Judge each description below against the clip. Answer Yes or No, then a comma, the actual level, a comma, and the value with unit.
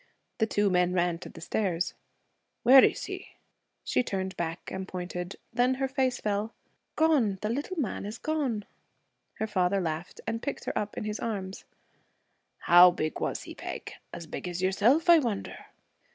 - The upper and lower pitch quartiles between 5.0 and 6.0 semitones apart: Yes, wide, 5.4 semitones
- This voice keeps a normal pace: Yes, average, 170 wpm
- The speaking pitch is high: Yes, high, 205 Hz